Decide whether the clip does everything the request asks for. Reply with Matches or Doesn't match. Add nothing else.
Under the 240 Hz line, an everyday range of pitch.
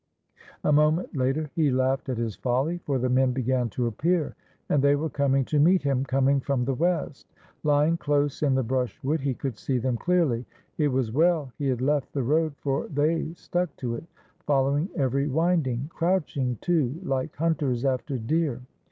Matches